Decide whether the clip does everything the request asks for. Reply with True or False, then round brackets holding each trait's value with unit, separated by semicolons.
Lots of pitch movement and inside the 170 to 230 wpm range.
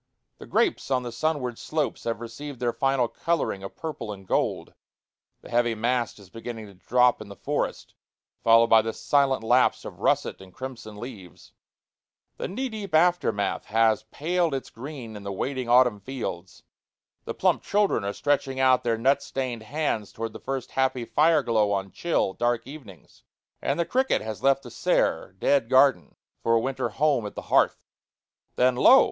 False (3.8 semitones; 175 wpm)